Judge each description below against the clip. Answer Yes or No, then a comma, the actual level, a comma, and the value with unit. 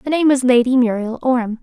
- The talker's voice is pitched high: Yes, very high, 250 Hz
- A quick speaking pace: Yes, fast, 220 wpm